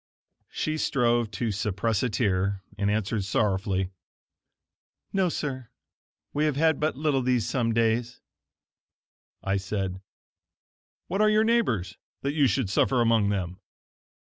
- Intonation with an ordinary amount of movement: No, wide, 5.8 semitones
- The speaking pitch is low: Yes, low, 115 Hz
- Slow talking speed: Yes, slow, 130 wpm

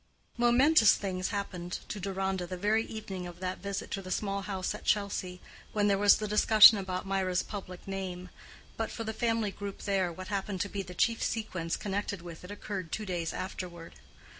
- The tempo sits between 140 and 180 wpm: No, average, 190 wpm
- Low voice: No, high, 195 Hz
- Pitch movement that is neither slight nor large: No, narrow, 2.2 semitones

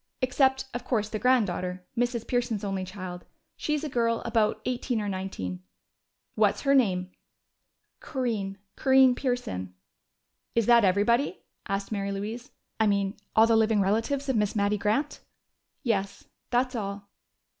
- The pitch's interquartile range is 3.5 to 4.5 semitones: Yes, average, 3.8 semitones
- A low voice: No, high, 220 Hz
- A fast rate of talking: No, average, 140 wpm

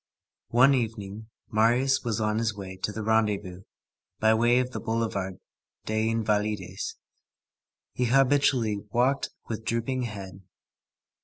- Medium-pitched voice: No, low, 110 Hz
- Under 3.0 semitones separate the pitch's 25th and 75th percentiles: Yes, narrow, 2.6 semitones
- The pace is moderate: No, slow, 125 wpm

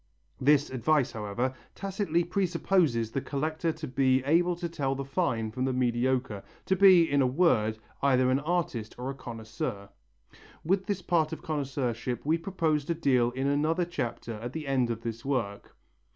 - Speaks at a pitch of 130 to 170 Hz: Yes, low, 135 Hz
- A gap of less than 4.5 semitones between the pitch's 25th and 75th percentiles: No, average, 5.3 semitones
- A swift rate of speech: No, average, 170 wpm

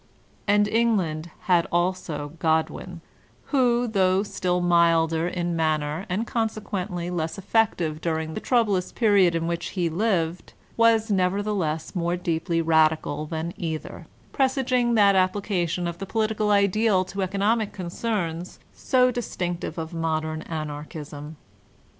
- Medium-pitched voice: Yes, medium, 180 Hz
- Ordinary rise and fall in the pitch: Yes, average, 4.2 semitones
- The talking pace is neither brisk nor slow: No, slow, 130 wpm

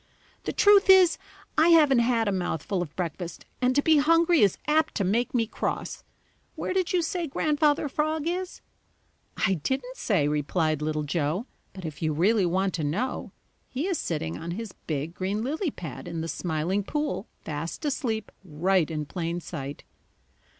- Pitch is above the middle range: Yes, high, 200 Hz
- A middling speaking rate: Yes, average, 170 wpm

